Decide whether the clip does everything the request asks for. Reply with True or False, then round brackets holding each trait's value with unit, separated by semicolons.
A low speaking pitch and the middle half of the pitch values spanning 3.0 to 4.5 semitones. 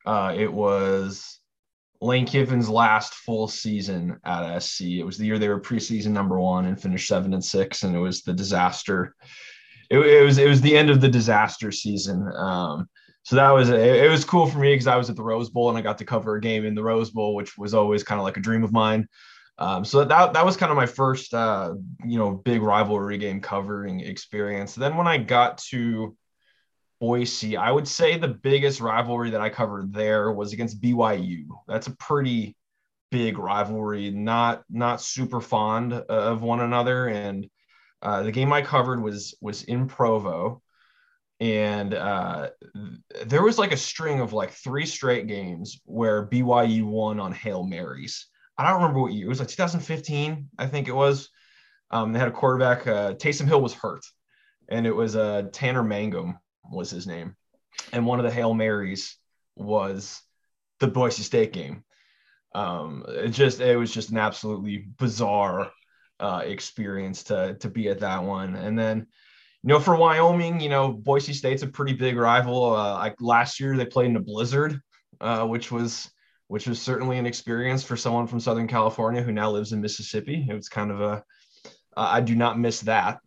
True (115 Hz; 3.7 semitones)